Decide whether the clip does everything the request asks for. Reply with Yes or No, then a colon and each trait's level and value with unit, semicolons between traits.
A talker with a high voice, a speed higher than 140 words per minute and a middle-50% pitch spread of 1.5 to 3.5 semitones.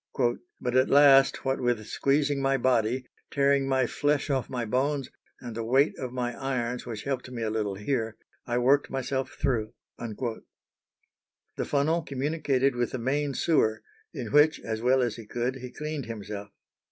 No: low, 130 Hz; average, 165 wpm; average, 2.8 semitones